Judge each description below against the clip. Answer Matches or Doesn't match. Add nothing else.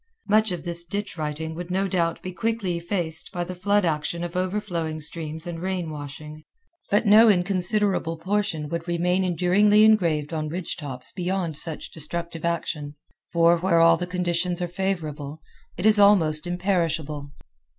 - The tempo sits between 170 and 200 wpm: Doesn't match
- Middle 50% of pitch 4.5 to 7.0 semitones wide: Doesn't match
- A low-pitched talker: Doesn't match